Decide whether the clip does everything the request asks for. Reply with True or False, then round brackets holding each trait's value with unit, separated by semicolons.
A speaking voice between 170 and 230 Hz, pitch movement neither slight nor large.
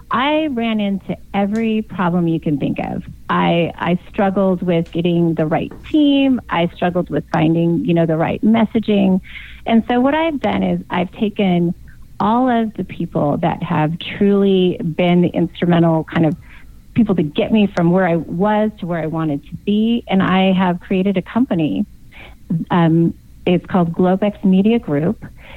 True (185 Hz; 3.8 semitones)